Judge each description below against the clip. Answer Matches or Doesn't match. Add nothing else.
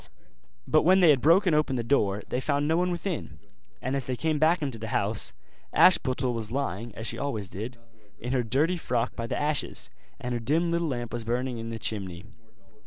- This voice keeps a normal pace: Doesn't match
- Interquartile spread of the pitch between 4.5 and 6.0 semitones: Matches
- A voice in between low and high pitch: Doesn't match